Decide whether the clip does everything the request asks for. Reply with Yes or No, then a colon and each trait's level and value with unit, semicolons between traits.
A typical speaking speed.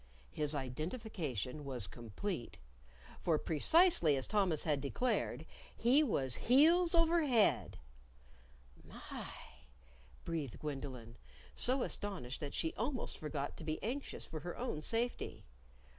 No: slow, 115 wpm